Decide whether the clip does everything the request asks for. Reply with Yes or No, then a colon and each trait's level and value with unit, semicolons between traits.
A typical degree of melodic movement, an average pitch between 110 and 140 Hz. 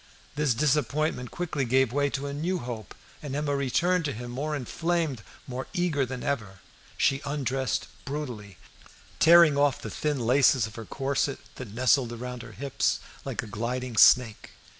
Yes: average, 3.3 semitones; low, 135 Hz